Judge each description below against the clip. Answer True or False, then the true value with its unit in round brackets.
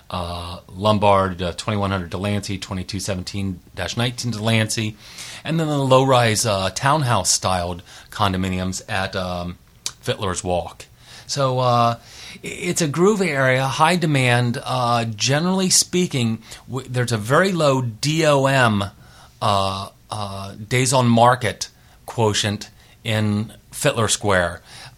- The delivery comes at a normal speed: False (115 wpm)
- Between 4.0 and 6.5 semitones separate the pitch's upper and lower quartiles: True (4.8 semitones)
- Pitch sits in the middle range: False (115 Hz)